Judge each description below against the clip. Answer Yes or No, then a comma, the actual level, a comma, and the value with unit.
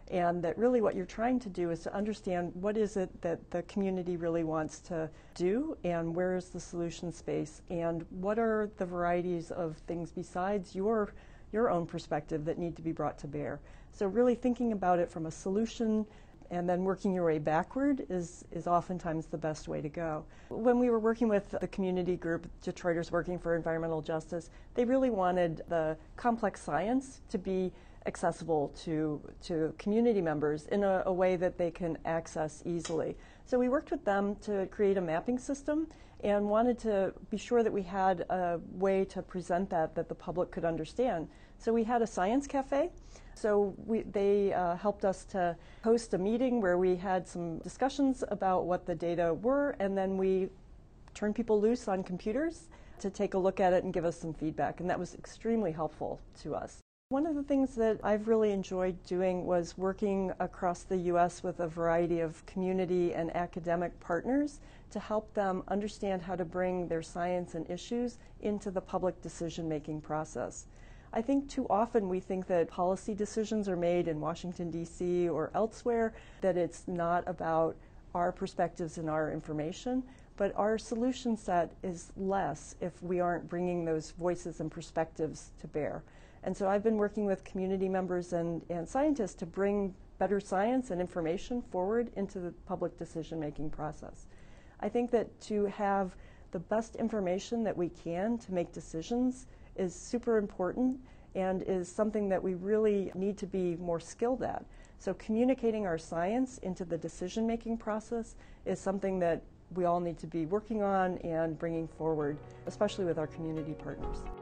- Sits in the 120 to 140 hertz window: No, medium, 185 Hz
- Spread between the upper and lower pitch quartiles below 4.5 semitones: Yes, average, 3.8 semitones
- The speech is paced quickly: No, average, 180 wpm